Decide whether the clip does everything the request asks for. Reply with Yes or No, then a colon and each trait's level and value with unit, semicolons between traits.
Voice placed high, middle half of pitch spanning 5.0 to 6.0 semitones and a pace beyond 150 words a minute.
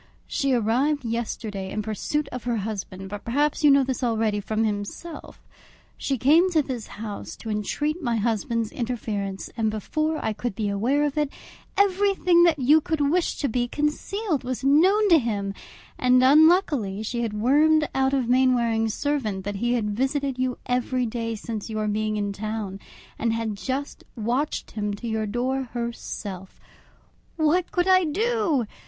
Yes: high, 245 Hz; average, 5.3 semitones; average, 165 wpm